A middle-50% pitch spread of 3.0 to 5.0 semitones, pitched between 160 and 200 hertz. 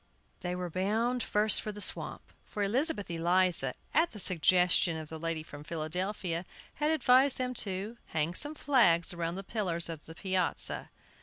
Yes: average, 4.7 semitones; medium, 185 Hz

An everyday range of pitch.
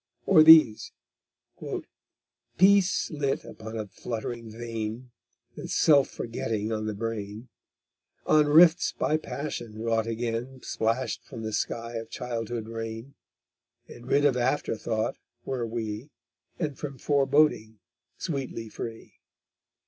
Yes: average, 3.9 semitones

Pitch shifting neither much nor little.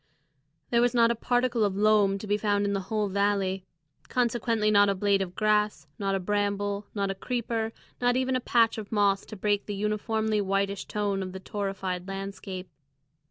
No: narrow, 1.9 semitones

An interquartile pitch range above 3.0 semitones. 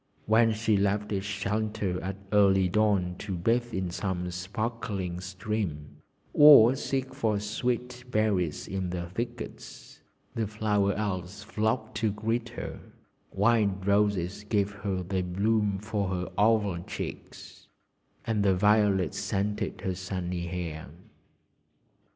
No: average, 2.7 semitones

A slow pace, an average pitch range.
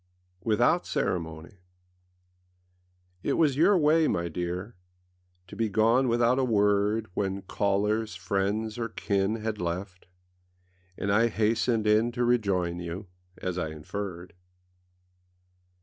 Yes: slow, 120 wpm; average, 3.9 semitones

